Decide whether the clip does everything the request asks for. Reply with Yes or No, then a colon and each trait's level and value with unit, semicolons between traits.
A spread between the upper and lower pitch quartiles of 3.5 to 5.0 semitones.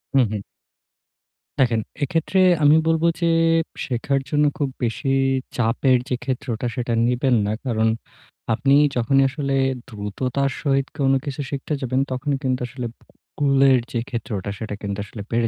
No: average, 2.9 semitones